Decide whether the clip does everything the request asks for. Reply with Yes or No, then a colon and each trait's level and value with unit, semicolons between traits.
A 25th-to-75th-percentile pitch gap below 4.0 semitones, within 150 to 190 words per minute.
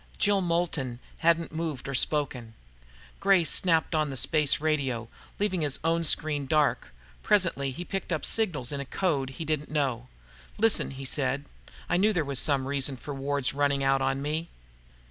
Yes: average, 3.6 semitones; average, 170 wpm